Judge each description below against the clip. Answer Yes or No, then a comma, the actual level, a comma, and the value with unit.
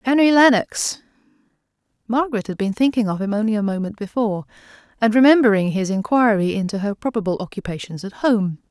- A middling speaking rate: Yes, average, 150 wpm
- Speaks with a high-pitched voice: Yes, high, 215 Hz